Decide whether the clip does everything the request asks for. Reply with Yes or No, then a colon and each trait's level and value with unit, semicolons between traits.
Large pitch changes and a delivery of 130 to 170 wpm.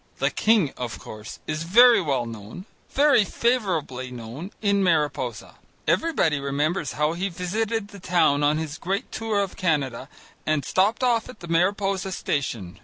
Yes: wide, 6.2 semitones; average, 155 wpm